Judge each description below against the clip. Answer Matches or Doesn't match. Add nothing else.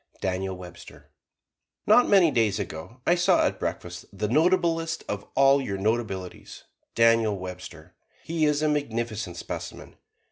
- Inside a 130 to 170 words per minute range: Matches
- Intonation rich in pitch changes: Matches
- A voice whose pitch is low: Matches